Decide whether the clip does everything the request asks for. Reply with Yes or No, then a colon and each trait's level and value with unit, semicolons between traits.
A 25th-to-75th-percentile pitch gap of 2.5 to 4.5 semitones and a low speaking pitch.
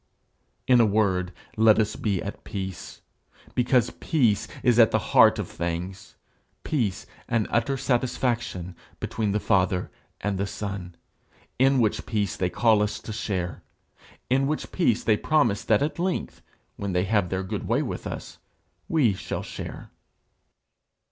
Yes: average, 4.2 semitones; low, 105 Hz